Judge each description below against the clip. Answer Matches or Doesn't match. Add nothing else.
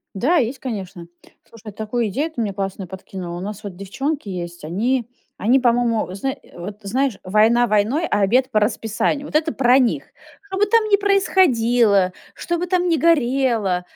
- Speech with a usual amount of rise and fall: Doesn't match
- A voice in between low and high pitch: Doesn't match